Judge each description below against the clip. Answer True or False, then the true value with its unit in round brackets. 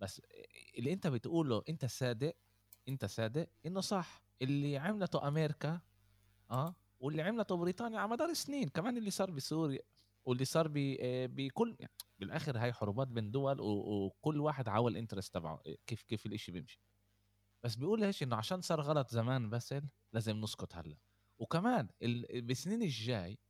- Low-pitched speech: True (130 Hz)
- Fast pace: True (145 wpm)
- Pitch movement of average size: False (7.3 semitones)